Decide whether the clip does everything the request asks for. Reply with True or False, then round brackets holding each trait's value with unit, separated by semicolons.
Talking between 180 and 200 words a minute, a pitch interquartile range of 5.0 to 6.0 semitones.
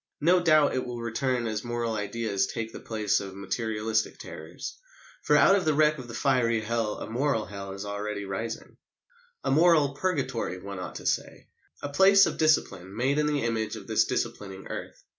True (190 wpm; 5.3 semitones)